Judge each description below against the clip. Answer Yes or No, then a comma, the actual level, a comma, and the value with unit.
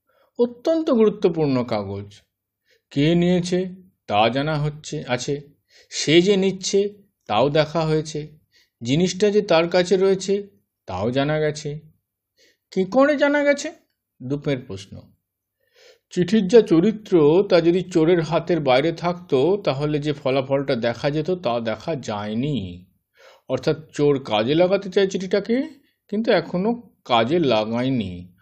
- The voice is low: No, medium, 160 Hz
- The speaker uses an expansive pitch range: Yes, wide, 7.3 semitones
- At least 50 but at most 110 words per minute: No, fast, 120 wpm